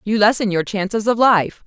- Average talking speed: No, fast, 215 wpm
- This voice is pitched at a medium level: No, high, 210 Hz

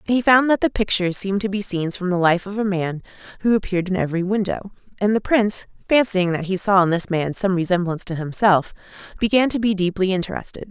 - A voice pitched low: No, high, 195 Hz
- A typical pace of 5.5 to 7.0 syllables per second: Yes, 6.4 syllables/s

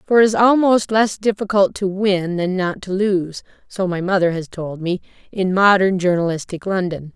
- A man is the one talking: No, female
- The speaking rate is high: No, average, 185 wpm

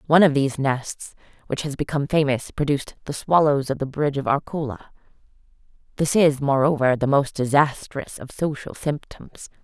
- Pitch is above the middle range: No, medium, 140 Hz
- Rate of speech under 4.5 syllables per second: No, 5.3 syllables/s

